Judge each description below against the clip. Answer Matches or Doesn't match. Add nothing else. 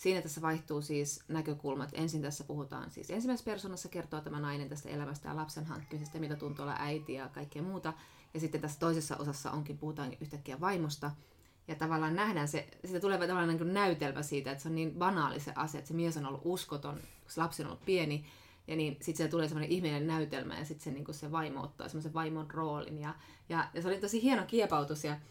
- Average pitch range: Doesn't match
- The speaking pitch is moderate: Matches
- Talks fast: Matches